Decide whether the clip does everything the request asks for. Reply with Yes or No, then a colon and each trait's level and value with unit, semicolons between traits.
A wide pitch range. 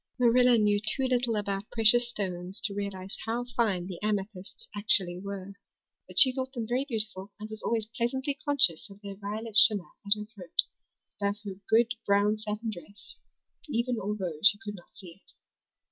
No: average, 2.8 semitones